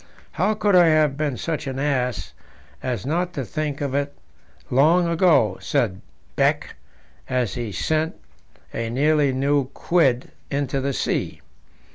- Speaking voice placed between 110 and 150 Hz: Yes, medium, 140 Hz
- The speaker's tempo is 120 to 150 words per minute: Yes, average, 140 wpm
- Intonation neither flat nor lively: Yes, average, 3.4 semitones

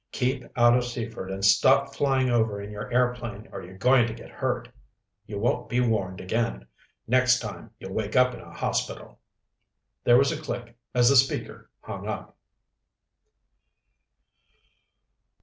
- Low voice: Yes, low, 120 Hz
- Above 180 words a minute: No, average, 150 wpm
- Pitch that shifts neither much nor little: Yes, average, 3.3 semitones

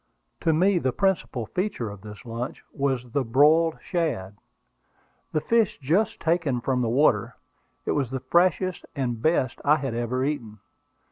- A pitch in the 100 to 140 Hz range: Yes, low, 135 Hz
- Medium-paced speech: Yes, average, 155 wpm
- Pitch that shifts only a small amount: No, wide, 5.5 semitones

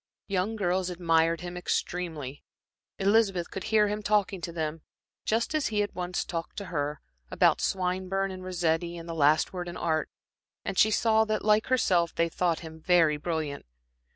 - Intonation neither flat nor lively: Yes, average, 3.3 semitones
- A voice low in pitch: No, medium, 180 Hz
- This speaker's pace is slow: No, average, 175 wpm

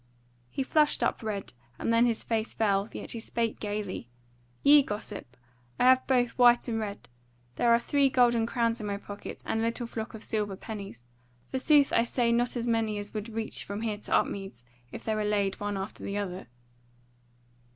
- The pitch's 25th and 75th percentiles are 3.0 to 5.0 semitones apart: No, narrow, 2.6 semitones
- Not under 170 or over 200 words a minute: Yes, average, 195 wpm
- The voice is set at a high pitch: Yes, high, 225 Hz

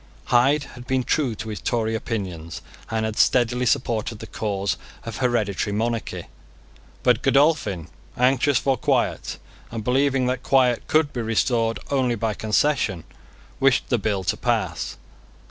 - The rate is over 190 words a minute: No, average, 145 wpm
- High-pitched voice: No, low, 120 Hz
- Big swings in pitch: No, average, 3.3 semitones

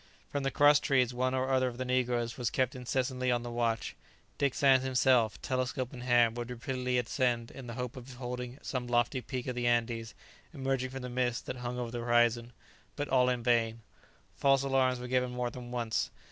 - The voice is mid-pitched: No, low, 125 Hz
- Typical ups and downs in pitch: No, narrow, 1.3 semitones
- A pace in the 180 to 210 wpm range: Yes, fast, 205 wpm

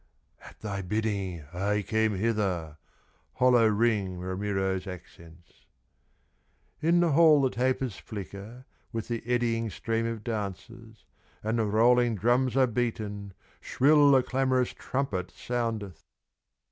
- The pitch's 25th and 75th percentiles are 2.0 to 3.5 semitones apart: No, average, 3.9 semitones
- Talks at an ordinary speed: No, slow, 120 wpm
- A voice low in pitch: Yes, low, 110 Hz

